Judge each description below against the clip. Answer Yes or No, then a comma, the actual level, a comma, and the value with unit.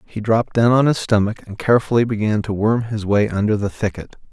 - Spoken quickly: Yes, fast, 220 wpm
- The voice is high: No, low, 110 Hz